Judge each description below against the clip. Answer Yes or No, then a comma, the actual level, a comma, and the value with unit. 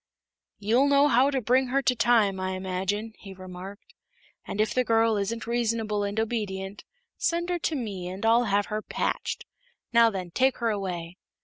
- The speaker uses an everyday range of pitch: Yes, average, 3.8 semitones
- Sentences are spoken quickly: No, average, 180 wpm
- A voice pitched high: Yes, high, 220 Hz